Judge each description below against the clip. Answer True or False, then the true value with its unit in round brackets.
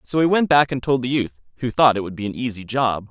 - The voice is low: True (125 Hz)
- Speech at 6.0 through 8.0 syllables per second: True (6.1 syllables/s)